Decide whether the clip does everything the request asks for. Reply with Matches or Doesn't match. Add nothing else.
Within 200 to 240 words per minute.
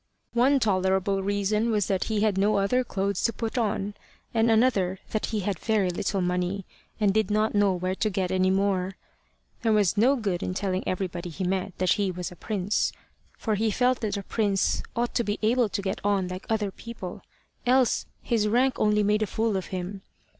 Matches